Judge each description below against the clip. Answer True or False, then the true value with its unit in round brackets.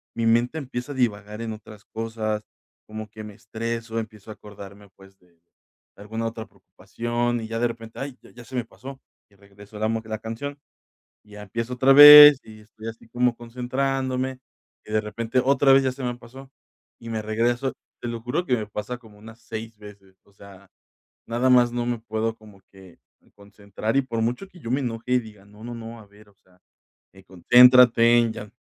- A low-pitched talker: True (115 Hz)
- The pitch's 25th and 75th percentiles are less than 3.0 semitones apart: True (2.5 semitones)